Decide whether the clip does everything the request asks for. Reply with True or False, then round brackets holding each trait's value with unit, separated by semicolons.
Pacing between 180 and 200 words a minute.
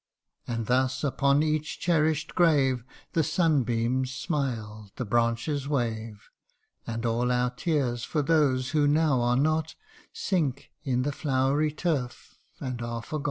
False (140 wpm)